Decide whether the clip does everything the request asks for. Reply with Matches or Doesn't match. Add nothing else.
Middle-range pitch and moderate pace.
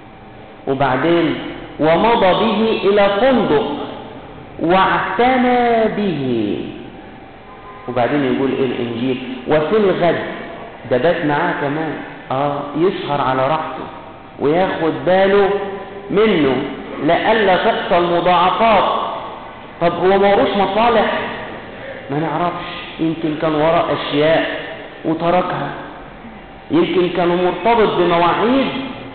Matches